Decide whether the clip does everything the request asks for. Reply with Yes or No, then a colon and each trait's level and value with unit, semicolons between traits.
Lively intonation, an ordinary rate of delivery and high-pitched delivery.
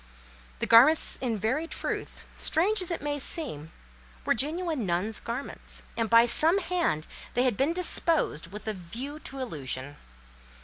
Yes: wide, 7.3 semitones; average, 150 wpm; very high, 255 Hz